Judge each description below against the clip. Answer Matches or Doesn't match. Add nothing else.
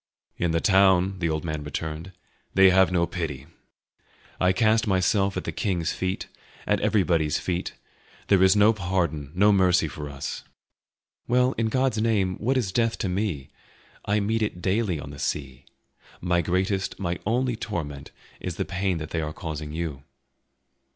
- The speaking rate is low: Doesn't match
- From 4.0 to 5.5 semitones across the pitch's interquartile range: Matches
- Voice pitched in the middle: Doesn't match